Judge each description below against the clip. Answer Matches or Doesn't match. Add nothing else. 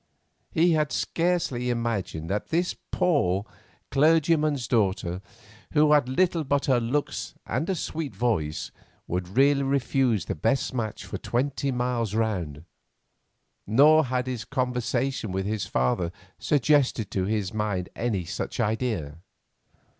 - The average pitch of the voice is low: Matches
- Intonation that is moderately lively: Doesn't match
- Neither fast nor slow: Doesn't match